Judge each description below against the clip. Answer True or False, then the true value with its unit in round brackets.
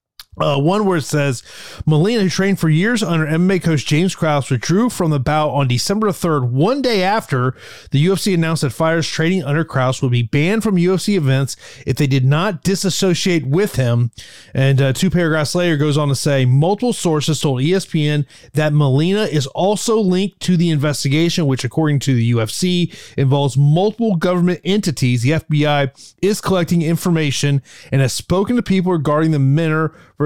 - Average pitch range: True (4.6 semitones)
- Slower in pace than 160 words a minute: False (175 wpm)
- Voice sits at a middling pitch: True (160 Hz)